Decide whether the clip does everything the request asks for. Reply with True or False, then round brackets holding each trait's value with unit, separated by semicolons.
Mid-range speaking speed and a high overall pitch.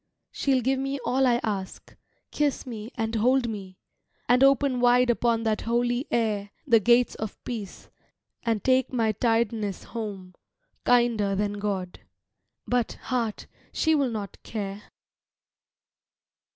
False (130 wpm; 230 Hz)